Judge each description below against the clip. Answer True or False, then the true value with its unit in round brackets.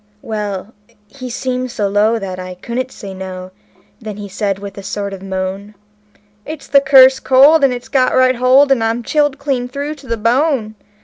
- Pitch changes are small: False (4.8 semitones)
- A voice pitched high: True (235 Hz)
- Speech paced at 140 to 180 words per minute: False (190 wpm)